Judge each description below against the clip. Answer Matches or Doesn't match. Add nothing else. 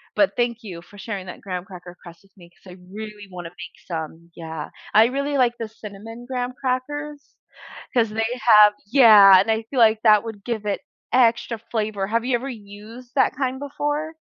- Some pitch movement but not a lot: Matches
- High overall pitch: Matches